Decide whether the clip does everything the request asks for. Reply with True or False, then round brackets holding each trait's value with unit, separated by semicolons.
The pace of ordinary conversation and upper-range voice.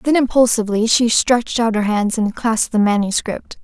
True (180 wpm; 225 Hz)